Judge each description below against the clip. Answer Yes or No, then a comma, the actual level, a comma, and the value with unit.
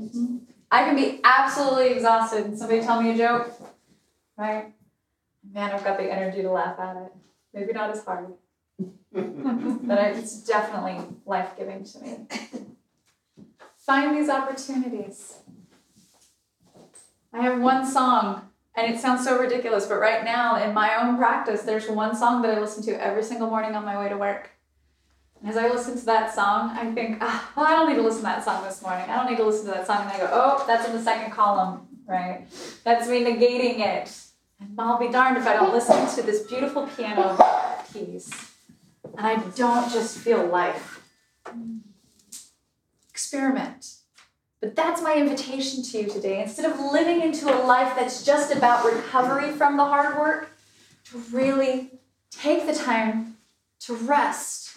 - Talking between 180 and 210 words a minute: No, average, 170 wpm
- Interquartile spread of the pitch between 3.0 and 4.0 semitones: Yes, average, 3.6 semitones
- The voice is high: Yes, high, 230 Hz